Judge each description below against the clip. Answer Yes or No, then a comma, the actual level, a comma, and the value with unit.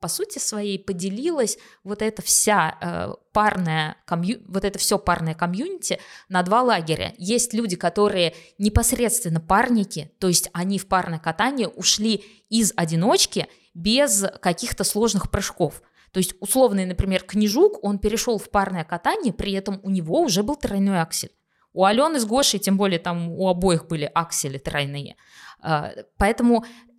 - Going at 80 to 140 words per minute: No, average, 150 wpm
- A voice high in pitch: Yes, high, 195 Hz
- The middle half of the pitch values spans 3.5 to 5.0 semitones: Yes, average, 4.1 semitones